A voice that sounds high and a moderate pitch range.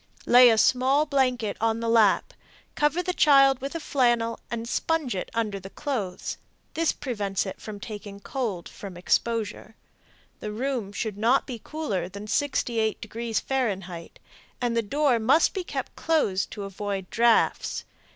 Yes: high, 230 Hz; average, 4.7 semitones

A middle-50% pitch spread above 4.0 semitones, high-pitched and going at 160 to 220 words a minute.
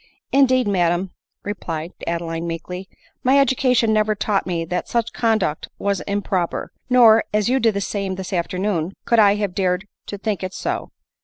No: average, 3.6 semitones; high, 200 Hz; average, 180 wpm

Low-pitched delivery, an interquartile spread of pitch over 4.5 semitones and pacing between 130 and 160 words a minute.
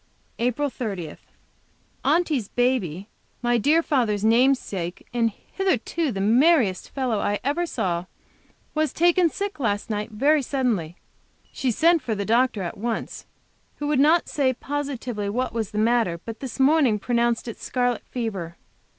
No: high, 240 Hz; average, 5.2 semitones; average, 150 wpm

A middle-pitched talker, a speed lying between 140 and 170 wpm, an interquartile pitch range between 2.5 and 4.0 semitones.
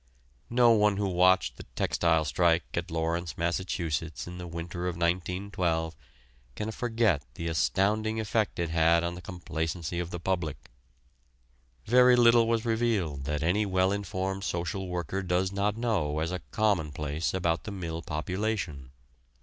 No: very low, 90 Hz; average, 150 wpm; average, 3.5 semitones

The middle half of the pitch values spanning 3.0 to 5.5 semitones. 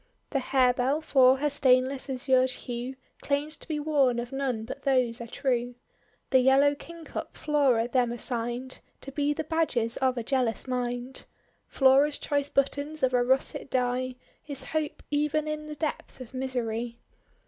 No: narrow, 2.6 semitones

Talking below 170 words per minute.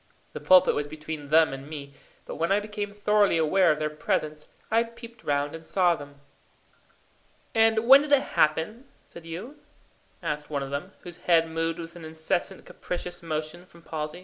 No: average, 180 wpm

